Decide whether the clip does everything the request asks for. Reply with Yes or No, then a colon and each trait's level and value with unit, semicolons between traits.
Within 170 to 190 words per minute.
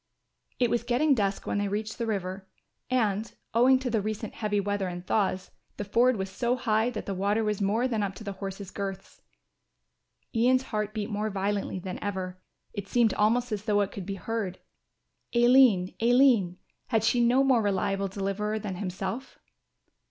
Yes: average, 180 wpm